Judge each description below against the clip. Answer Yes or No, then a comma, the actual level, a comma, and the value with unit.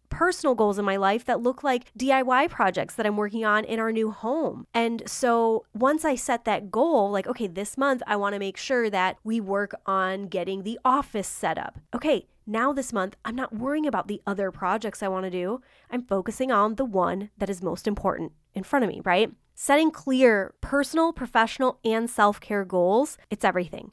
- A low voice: No, high, 225 Hz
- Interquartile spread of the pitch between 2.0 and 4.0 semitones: No, average, 4.4 semitones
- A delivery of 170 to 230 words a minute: Yes, fast, 205 wpm